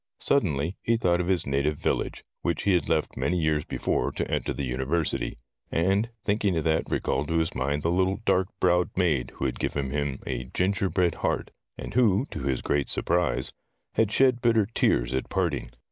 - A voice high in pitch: No, very low, 85 Hz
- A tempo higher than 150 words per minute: Yes, average, 190 wpm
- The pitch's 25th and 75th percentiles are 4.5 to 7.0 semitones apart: Yes, average, 5.1 semitones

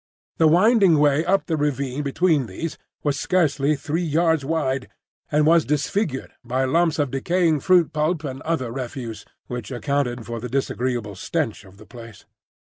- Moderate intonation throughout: Yes, average, 4.1 semitones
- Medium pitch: Yes, medium, 145 Hz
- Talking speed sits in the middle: Yes, average, 160 wpm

